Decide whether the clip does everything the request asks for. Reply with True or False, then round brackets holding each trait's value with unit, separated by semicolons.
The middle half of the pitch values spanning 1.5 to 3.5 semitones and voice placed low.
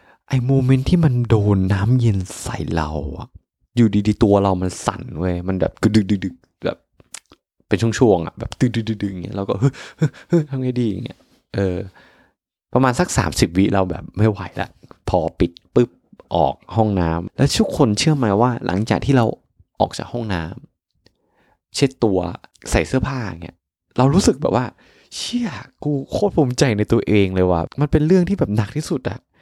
False (5.6 semitones; 115 Hz)